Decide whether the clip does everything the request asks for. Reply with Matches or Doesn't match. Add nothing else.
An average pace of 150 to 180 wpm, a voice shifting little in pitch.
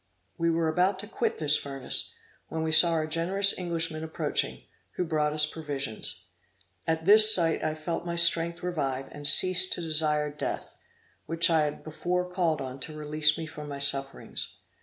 Matches